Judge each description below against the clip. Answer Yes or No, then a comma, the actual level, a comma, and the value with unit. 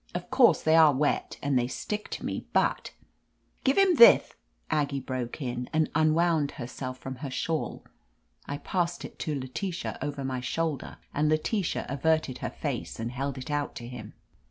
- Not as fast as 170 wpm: No, average, 185 wpm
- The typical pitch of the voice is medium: Yes, medium, 145 Hz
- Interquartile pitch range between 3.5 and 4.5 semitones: Yes, average, 4.0 semitones